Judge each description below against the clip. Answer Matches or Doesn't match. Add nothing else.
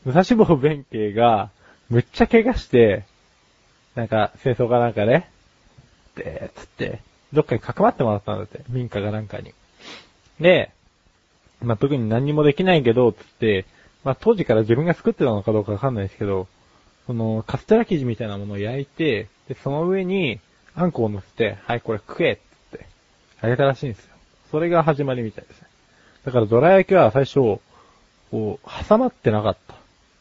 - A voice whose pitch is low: Matches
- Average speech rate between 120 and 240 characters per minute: Doesn't match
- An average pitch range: Doesn't match